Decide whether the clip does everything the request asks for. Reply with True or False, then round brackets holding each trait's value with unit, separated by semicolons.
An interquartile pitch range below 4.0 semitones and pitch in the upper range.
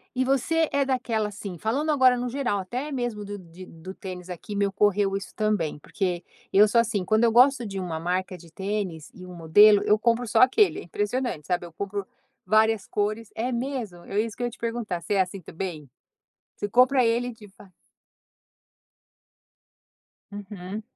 False (4.4 semitones; 210 Hz)